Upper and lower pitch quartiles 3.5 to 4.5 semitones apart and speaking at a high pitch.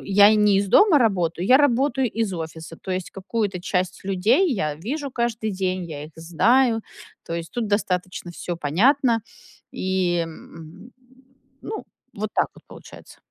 No: average, 5.1 semitones; high, 195 Hz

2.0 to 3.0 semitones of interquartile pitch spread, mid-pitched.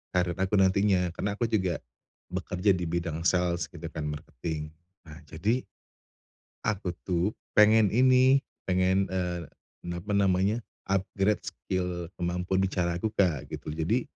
No: average, 2.7 semitones; very low, 90 Hz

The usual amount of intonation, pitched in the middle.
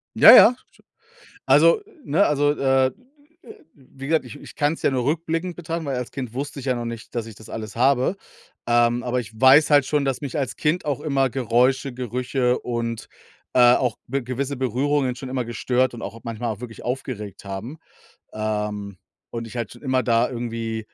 No: average, 3.0 semitones; low, 125 Hz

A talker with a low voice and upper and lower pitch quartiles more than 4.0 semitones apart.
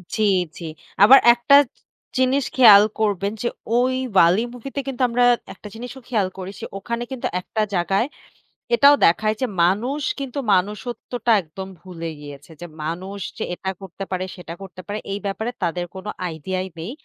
No: high, 205 Hz; average, 4.8 semitones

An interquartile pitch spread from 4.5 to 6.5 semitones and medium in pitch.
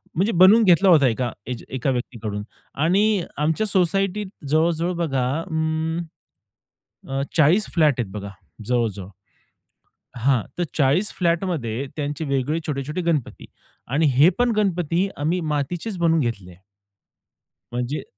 Yes: average, 5.2 semitones; medium, 155 Hz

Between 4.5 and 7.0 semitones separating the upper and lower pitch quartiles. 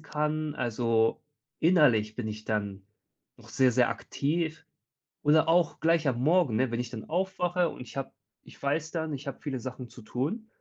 Yes: average, 5.3 semitones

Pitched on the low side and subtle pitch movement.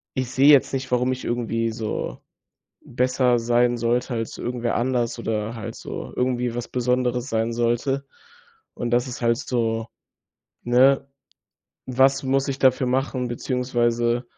Yes: low, 125 Hz; narrow, 1.5 semitones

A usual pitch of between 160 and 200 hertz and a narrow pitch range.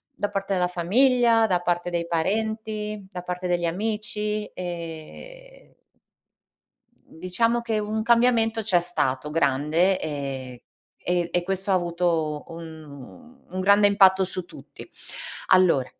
No: medium, 185 Hz; average, 4.2 semitones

